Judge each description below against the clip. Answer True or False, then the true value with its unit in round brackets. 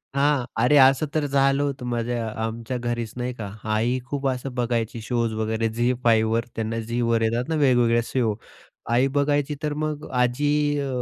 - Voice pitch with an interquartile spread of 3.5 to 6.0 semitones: False (3.1 semitones)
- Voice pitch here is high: False (120 Hz)